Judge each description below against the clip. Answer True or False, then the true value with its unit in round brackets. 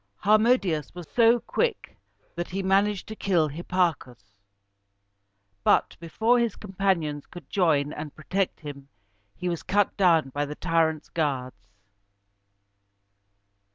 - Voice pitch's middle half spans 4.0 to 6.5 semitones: True (4.9 semitones)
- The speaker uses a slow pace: True (120 wpm)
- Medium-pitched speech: True (170 Hz)